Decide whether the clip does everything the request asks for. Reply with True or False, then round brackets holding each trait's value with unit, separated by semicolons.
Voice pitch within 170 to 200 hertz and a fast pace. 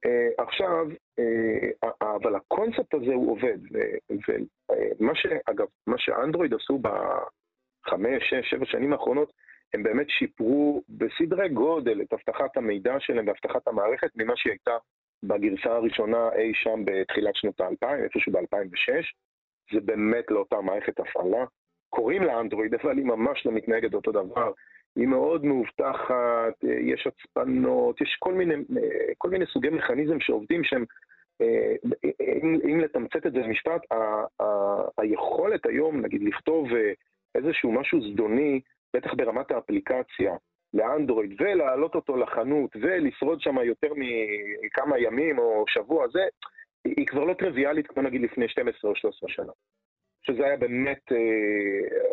False (190 Hz; 130 wpm)